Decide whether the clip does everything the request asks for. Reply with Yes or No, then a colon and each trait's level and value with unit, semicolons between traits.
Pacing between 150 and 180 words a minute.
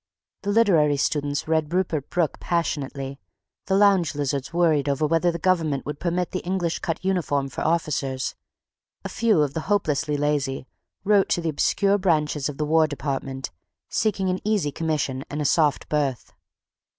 Yes: average, 165 wpm